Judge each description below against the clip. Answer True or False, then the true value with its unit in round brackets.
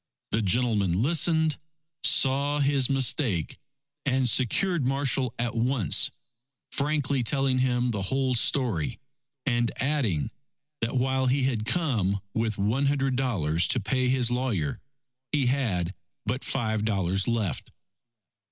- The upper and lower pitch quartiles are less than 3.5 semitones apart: False (3.8 semitones)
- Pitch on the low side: True (125 Hz)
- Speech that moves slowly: True (125 wpm)